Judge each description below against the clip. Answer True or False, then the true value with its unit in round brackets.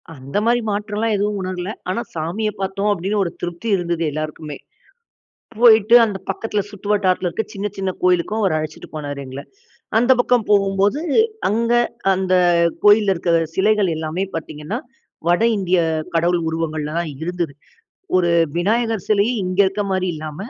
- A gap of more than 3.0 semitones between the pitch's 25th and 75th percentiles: True (3.7 semitones)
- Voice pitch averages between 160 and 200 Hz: True (190 Hz)